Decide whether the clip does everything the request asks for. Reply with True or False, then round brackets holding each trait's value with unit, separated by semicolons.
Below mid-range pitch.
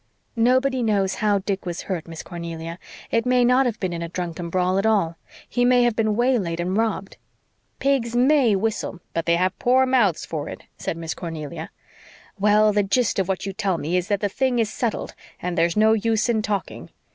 False (200 Hz)